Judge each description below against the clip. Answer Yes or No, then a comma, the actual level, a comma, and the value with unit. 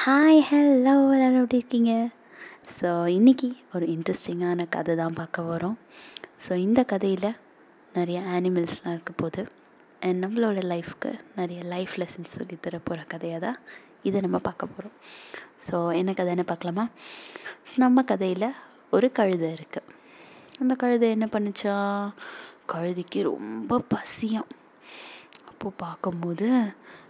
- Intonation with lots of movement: Yes, wide, 5.7 semitones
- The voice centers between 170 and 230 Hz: Yes, high, 190 Hz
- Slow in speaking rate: No, average, 115 wpm